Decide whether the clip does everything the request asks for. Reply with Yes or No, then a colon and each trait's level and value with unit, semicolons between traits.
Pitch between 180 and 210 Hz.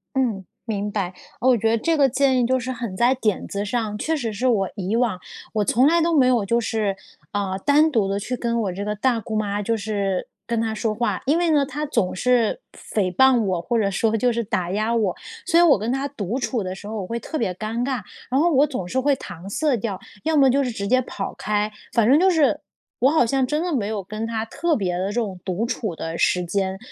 No: high, 230 Hz